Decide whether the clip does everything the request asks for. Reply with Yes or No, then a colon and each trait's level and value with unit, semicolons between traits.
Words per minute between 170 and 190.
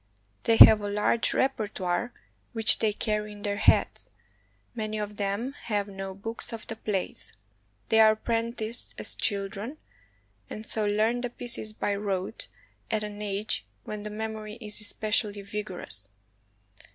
No: average, 155 wpm